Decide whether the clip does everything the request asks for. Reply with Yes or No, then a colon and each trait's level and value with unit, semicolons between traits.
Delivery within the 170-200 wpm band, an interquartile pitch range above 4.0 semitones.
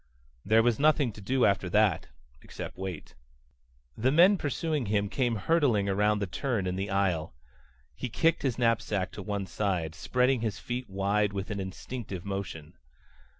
No: average, 160 wpm; average, 4.4 semitones